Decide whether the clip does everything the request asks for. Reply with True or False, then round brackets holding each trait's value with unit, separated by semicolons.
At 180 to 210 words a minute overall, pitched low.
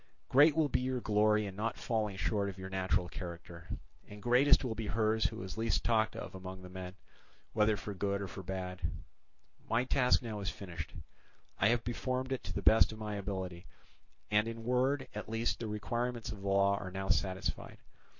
True (200 wpm; 105 Hz)